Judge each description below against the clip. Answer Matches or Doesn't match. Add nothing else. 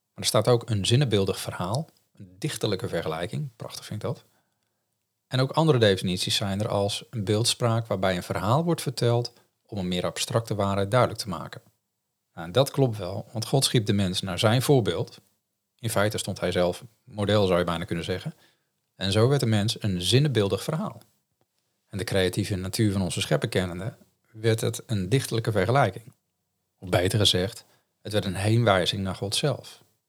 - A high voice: Doesn't match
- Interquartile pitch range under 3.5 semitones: Doesn't match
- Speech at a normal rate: Matches